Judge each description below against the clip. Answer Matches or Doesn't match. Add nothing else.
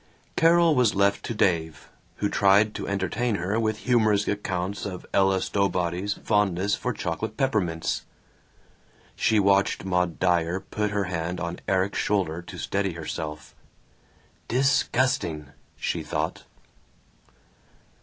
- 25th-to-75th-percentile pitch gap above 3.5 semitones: Doesn't match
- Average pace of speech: Doesn't match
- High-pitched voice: Doesn't match